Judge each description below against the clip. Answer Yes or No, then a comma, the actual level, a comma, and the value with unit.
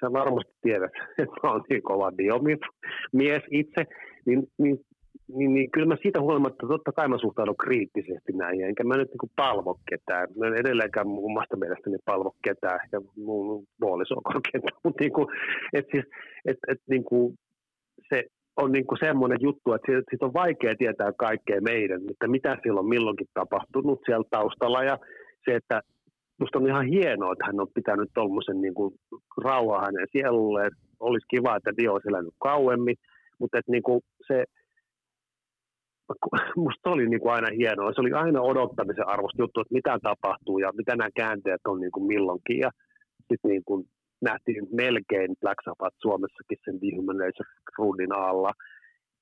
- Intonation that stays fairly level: No, average, 5.0 semitones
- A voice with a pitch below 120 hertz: No, low, 125 Hz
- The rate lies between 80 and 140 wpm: No, fast, 155 wpm